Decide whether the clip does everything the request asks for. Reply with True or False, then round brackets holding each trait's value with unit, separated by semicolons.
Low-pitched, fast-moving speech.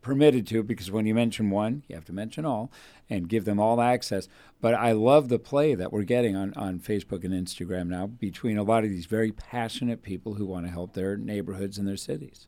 True (105 Hz; 230 wpm)